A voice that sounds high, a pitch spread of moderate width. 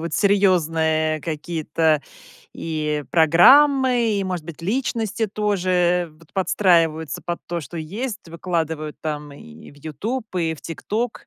No: medium, 170 Hz; average, 4.4 semitones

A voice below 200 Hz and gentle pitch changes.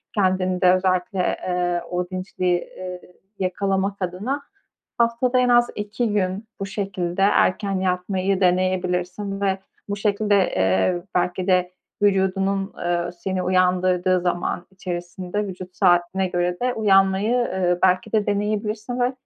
Yes: medium, 185 Hz; narrow, 2.1 semitones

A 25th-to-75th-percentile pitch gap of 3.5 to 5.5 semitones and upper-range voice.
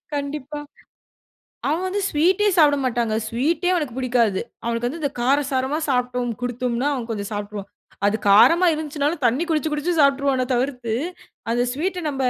Yes: average, 3.9 semitones; very high, 265 Hz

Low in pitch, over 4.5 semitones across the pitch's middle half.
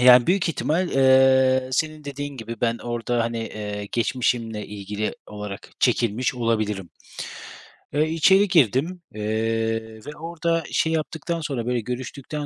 Yes: low, 125 Hz; average, 5.0 semitones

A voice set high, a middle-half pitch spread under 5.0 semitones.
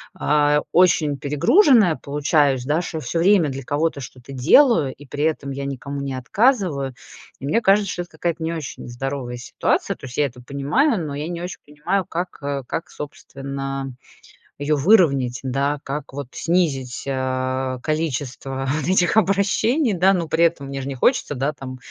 No: medium, 145 Hz; average, 4.2 semitones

